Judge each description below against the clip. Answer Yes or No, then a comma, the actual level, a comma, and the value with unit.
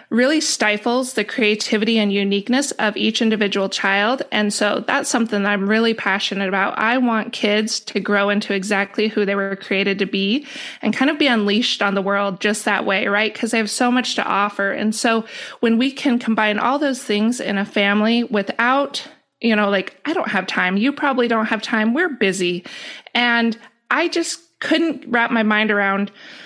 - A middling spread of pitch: Yes, average, 3.6 semitones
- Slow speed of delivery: No, average, 195 wpm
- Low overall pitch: No, high, 220 Hz